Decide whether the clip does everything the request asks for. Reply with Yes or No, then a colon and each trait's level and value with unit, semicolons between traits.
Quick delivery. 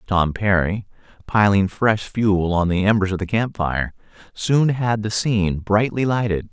No: average, 165 wpm